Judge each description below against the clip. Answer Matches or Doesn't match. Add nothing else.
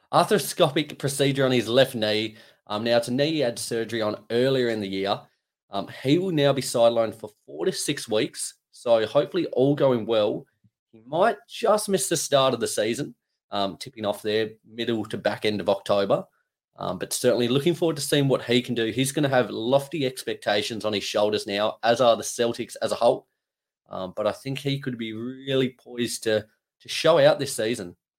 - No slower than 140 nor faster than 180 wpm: Doesn't match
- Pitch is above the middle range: Doesn't match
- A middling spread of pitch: Matches